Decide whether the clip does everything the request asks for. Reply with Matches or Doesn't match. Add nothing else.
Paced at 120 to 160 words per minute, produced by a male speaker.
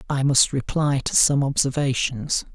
Matches